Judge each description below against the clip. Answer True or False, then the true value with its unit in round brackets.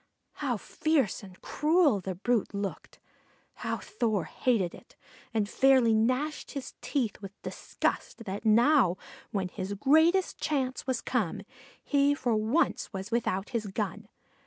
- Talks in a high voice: True (230 Hz)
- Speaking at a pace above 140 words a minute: False (135 wpm)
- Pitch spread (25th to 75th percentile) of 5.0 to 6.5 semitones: True (5.3 semitones)